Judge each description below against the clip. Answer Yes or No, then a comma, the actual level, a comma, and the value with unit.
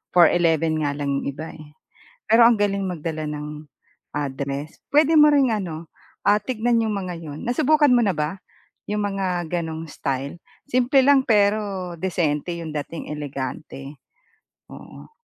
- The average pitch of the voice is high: No, medium, 175 Hz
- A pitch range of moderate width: No, wide, 6.2 semitones